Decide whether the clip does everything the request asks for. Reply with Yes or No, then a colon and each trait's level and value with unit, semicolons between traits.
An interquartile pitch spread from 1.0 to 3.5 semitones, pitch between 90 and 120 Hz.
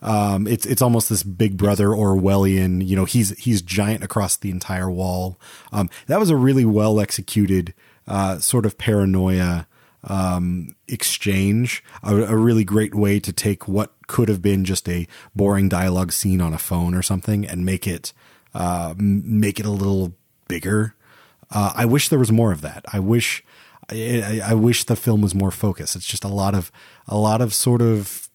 Yes: average, 2.8 semitones; low, 100 Hz